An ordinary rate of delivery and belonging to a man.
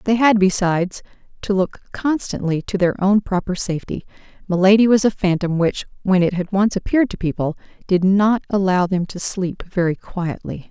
No: average, 175 wpm; female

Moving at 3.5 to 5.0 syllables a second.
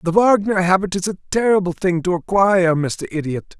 No: 5.4 syllables/s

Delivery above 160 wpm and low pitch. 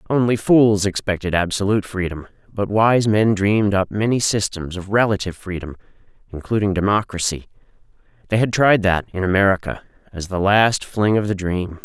No: average, 150 wpm; low, 100 Hz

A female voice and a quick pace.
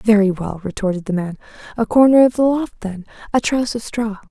Yes: female; fast, 210 wpm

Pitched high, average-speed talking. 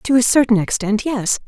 Yes: high, 230 Hz; average, 165 wpm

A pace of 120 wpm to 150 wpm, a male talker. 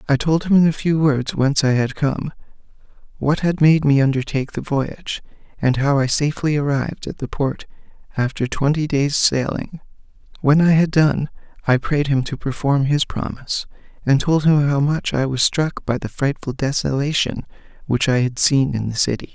No: average, 185 wpm; male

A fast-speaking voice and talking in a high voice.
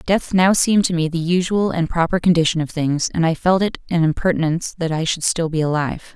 No: fast, 235 wpm; medium, 170 Hz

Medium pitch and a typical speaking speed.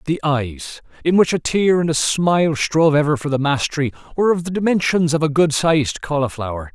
Yes: medium, 155 Hz; average, 195 wpm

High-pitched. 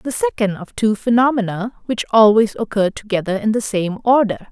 Yes: high, 215 Hz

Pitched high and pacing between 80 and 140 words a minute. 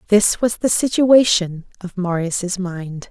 Yes: high, 195 Hz; slow, 135 wpm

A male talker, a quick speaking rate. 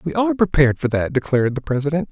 Yes: male; fast, 225 wpm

